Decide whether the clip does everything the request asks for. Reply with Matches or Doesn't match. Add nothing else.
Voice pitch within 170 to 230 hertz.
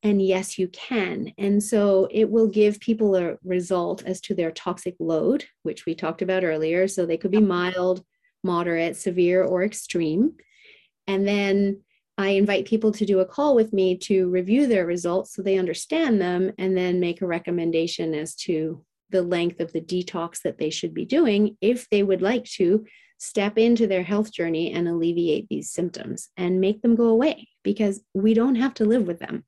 Matches